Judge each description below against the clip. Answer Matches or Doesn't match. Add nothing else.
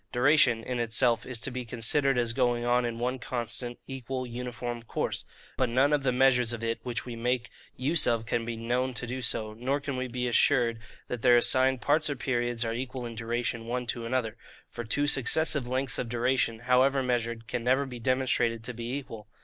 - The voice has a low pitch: Matches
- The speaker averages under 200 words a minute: Doesn't match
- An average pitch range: Doesn't match